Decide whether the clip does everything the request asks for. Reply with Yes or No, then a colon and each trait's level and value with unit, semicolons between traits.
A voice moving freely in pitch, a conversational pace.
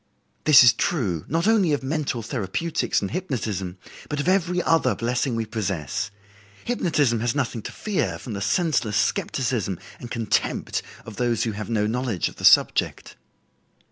Yes: wide, 6.1 semitones; average, 160 wpm